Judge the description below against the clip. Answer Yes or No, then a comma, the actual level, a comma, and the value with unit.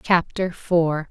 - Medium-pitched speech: Yes, medium, 170 Hz